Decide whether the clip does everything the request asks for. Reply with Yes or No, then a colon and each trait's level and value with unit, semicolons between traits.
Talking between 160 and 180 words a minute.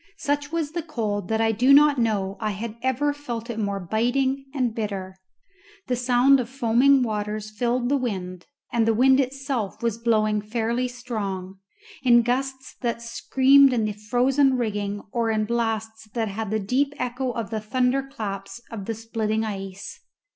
Yes: average, 170 wpm